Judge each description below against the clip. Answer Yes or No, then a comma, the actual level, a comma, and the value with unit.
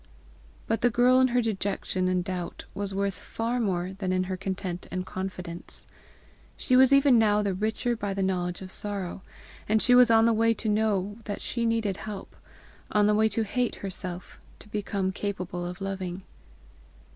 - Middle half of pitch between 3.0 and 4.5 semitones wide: Yes, average, 3.3 semitones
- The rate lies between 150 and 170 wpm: No, average, 180 wpm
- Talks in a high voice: Yes, high, 200 Hz